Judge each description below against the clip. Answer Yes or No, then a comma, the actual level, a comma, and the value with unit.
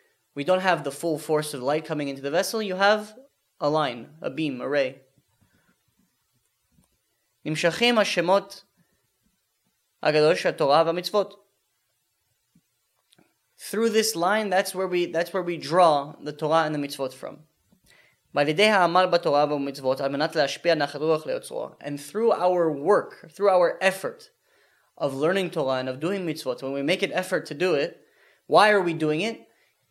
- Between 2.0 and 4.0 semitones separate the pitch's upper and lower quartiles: No, wide, 5.5 semitones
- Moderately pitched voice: Yes, medium, 170 Hz